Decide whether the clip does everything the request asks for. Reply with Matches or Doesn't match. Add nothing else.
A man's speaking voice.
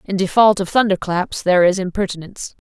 Doesn't match